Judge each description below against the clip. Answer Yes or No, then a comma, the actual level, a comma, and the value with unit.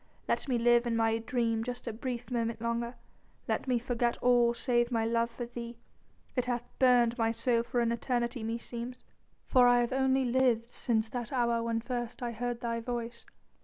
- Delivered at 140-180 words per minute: No, average, 190 wpm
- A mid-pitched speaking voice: No, high, 240 Hz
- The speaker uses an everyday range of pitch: No, narrow, 1.0 semitones